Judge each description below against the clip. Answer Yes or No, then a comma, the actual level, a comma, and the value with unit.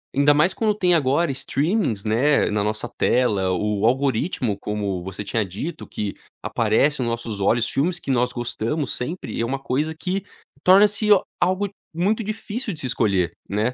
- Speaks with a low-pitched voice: Yes, low, 130 Hz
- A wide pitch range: Yes, wide, 8.1 semitones